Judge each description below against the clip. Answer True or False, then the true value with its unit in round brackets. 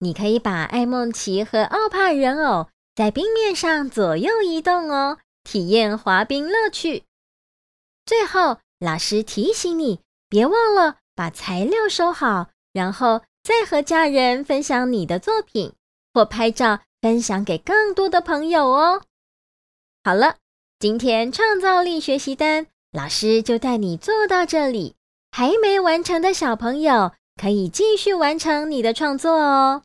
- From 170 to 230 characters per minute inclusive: True (210 characters per minute)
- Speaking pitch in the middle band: False (275 Hz)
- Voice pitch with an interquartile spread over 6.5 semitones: True (8.3 semitones)